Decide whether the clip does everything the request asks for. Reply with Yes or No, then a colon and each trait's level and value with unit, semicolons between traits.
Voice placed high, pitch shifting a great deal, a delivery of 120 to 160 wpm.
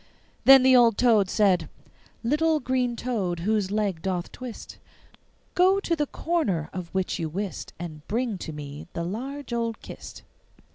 Yes: high, 220 Hz; wide, 6.1 semitones; average, 155 wpm